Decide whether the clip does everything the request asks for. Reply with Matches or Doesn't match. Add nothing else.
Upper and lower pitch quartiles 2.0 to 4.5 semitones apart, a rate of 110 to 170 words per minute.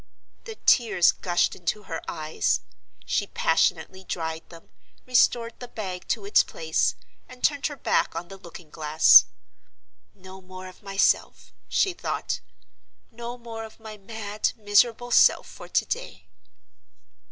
Doesn't match